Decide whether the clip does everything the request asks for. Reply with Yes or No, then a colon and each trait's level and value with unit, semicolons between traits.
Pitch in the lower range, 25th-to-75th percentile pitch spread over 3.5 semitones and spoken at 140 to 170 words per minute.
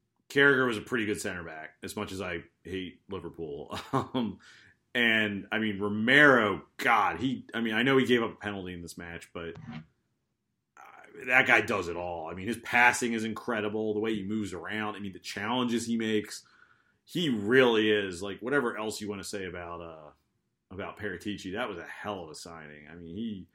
No: low, 105 Hz; average, 4.1 semitones; fast, 205 wpm